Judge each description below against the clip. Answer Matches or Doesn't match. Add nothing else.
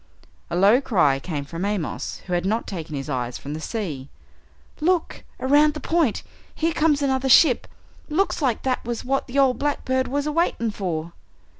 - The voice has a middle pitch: Doesn't match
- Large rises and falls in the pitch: Matches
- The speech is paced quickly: Doesn't match